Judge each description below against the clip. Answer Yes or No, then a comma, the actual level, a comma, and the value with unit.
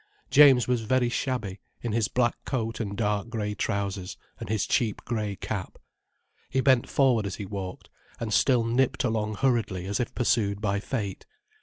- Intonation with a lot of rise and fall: No, average, 3.4 semitones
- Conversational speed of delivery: Yes, average, 170 wpm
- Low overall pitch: Yes, low, 110 Hz